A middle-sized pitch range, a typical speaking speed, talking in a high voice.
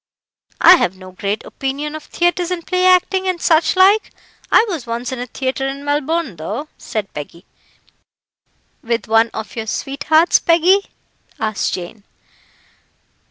No: wide, 7.7 semitones; average, 145 wpm; very high, 275 Hz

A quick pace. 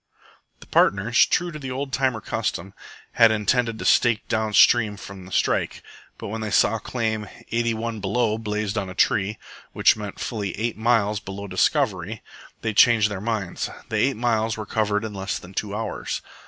No: average, 180 wpm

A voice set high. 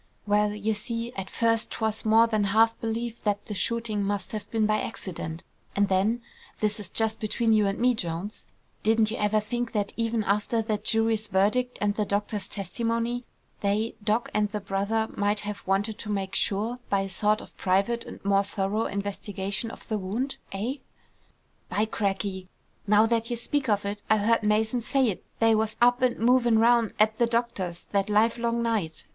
Yes: high, 215 Hz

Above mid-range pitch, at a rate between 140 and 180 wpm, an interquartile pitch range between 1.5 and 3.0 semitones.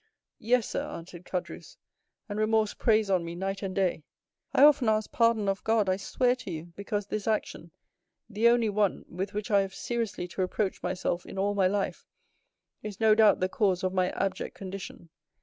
No: high, 200 Hz; average, 190 wpm; average, 2.7 semitones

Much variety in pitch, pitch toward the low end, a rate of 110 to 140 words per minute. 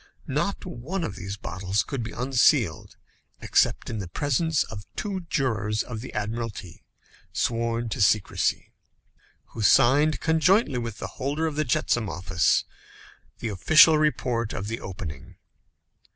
Yes: wide, 6.0 semitones; low, 115 Hz; slow, 135 wpm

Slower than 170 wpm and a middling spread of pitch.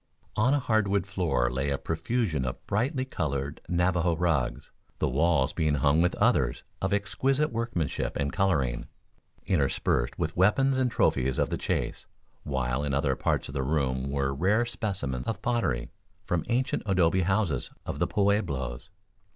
No: average, 155 wpm; wide, 7.1 semitones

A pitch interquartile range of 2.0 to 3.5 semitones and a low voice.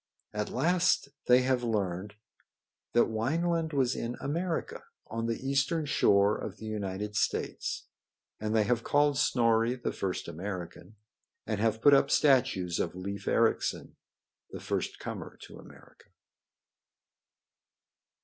No: average, 4.9 semitones; low, 115 Hz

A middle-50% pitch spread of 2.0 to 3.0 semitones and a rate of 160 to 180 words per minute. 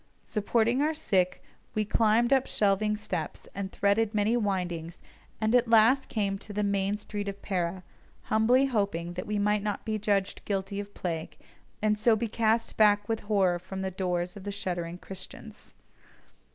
Yes: narrow, 2.4 semitones; average, 175 wpm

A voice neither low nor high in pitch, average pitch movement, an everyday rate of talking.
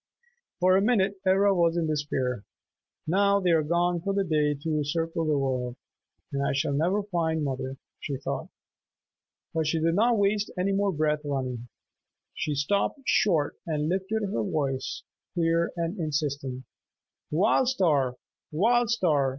Yes: medium, 165 Hz; average, 5.0 semitones; average, 150 wpm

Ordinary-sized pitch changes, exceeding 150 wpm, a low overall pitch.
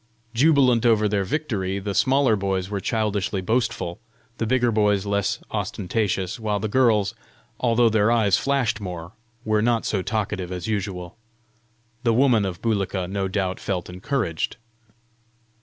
No: average, 3.3 semitones; average, 140 wpm; low, 105 Hz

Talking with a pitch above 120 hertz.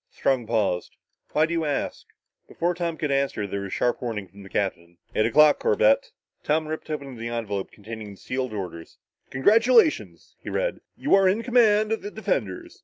Yes: medium, 140 Hz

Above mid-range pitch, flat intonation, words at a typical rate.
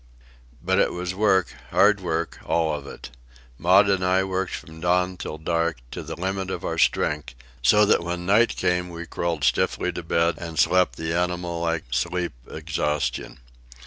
No: very low, 85 Hz; narrow, 2.1 semitones; average, 175 wpm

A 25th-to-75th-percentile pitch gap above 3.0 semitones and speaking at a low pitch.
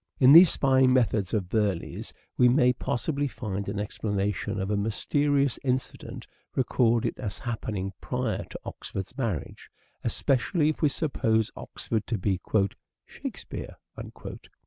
Yes: average, 4.4 semitones; low, 115 Hz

